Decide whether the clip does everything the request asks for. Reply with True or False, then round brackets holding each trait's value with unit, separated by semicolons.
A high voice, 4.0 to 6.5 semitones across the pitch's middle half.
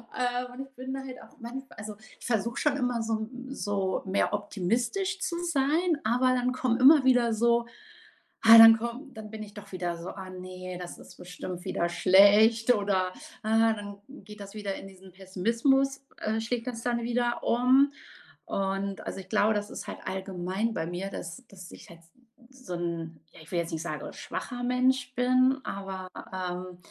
True (220 Hz; 4.8 semitones)